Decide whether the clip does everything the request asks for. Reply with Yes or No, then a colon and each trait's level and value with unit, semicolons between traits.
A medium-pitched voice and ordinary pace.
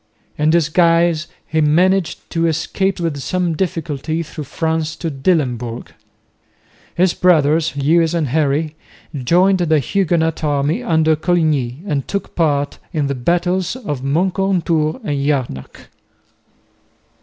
No: medium, 160 Hz; slow, 120 wpm